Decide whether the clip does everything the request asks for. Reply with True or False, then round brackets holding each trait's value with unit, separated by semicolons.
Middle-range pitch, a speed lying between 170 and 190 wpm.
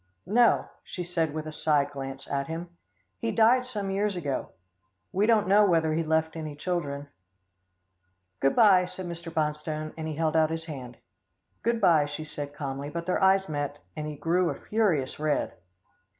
True (160 Hz; 180 wpm)